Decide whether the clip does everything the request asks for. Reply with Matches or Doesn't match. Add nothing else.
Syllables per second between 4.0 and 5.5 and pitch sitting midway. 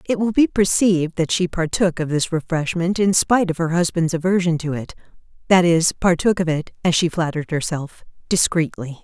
Matches